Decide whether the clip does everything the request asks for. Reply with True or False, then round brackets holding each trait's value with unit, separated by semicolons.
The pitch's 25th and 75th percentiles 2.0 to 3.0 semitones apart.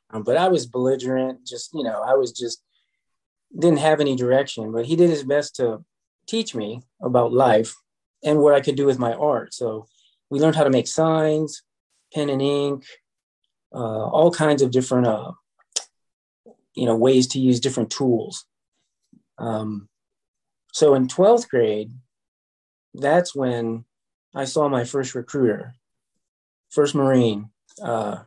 False (3.9 semitones)